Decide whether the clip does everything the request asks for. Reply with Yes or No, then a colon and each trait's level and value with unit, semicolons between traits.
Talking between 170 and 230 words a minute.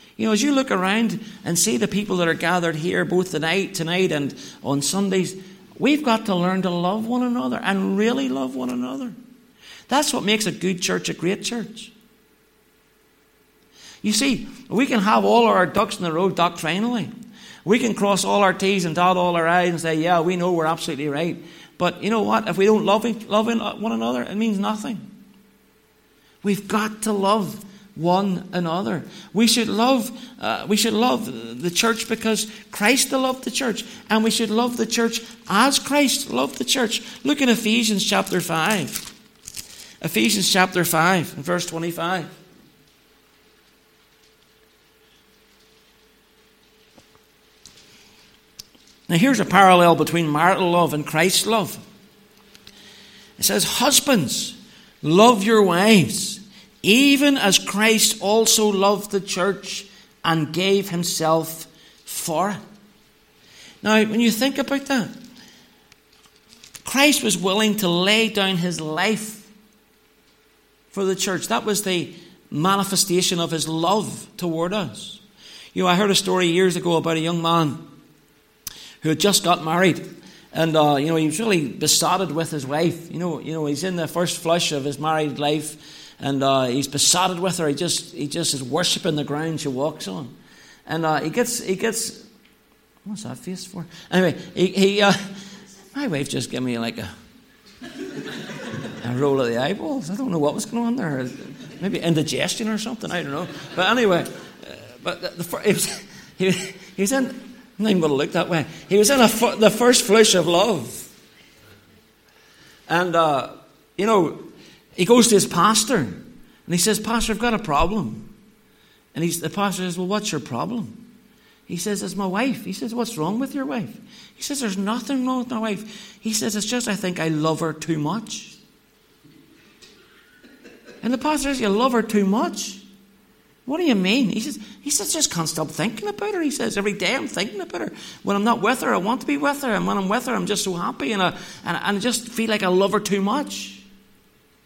Yes: average, 180 wpm